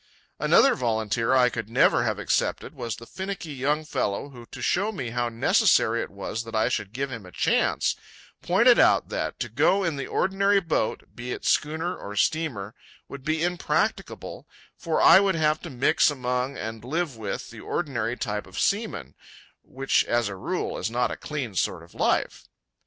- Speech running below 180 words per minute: No, average, 185 wpm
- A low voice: Yes, low, 130 Hz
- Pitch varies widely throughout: Yes, wide, 5.9 semitones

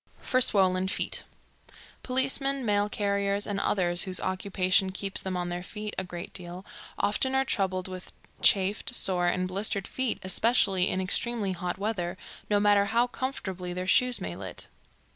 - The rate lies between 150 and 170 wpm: Yes, average, 160 wpm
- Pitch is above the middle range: Yes, high, 195 Hz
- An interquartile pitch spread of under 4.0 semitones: Yes, narrow, 2.4 semitones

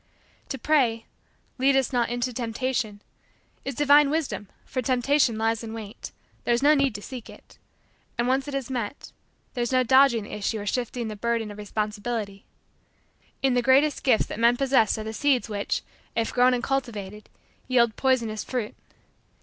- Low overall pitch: No, high, 240 Hz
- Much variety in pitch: No, average, 3.3 semitones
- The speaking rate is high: No, average, 180 wpm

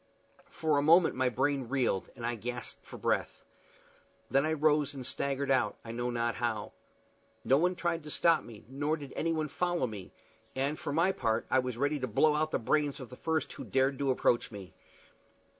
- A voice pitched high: No, low, 135 Hz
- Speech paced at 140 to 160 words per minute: No, average, 200 wpm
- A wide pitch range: No, average, 4.0 semitones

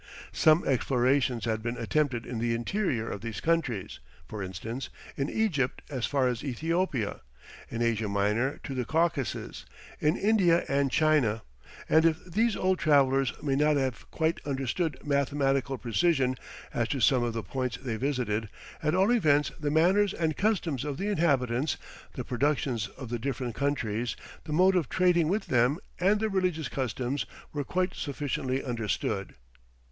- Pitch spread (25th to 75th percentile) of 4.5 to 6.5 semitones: Yes, average, 5.0 semitones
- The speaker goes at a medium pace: Yes, average, 160 wpm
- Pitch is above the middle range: No, low, 135 Hz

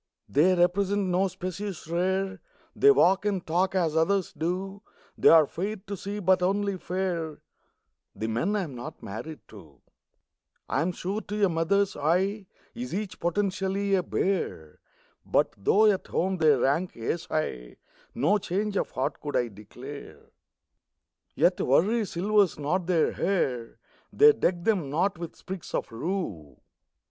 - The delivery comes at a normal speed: Yes, average, 150 wpm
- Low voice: No, medium, 185 Hz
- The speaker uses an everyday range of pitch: Yes, average, 4.1 semitones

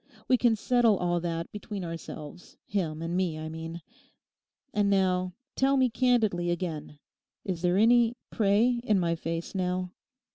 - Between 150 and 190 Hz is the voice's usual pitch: Yes, medium, 185 Hz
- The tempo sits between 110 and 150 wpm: Yes, average, 140 wpm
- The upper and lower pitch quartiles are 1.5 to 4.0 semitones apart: No, average, 4.4 semitones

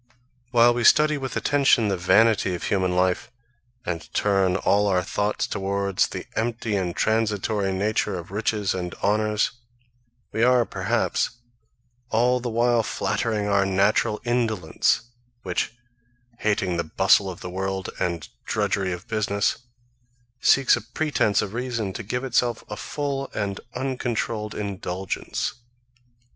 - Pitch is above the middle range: No, low, 105 Hz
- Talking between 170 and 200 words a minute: No, slow, 135 wpm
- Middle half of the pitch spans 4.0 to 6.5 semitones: No, average, 3.5 semitones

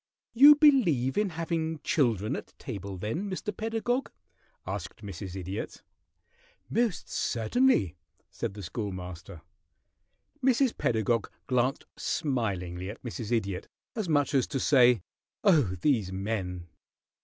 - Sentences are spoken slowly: Yes, slow, 115 wpm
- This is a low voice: Yes, low, 120 Hz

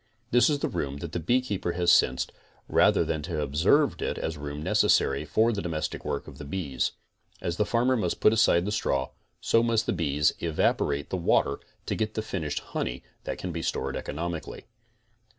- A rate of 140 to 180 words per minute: No, average, 195 wpm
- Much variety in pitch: Yes, wide, 6.6 semitones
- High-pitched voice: No, very low, 85 Hz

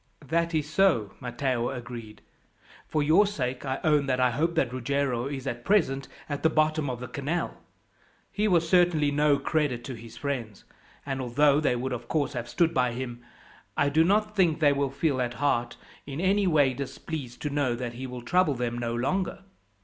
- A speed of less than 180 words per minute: No, average, 195 wpm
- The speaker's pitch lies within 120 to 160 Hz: Yes, medium, 140 Hz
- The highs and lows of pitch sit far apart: No, average, 4.3 semitones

